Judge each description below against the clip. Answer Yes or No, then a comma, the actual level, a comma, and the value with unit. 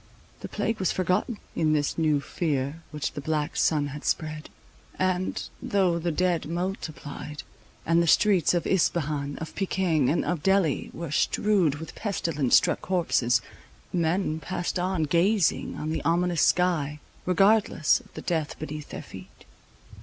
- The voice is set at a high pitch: No, medium, 165 Hz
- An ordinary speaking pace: Yes, average, 150 wpm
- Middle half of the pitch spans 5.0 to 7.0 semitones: No, average, 3.3 semitones